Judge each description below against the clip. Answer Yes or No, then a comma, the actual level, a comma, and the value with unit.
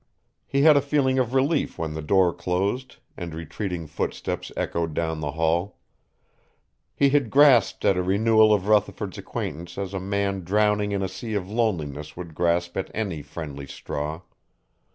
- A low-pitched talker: Yes, very low, 95 Hz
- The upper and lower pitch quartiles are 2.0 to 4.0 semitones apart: No, average, 4.9 semitones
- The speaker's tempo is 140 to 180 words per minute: Yes, average, 165 wpm